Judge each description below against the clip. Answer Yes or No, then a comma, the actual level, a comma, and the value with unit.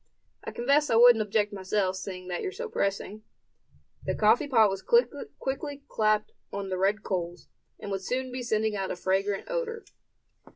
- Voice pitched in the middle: No, high, 215 Hz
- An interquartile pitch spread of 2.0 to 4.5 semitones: No, average, 5.1 semitones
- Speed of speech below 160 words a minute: No, average, 170 wpm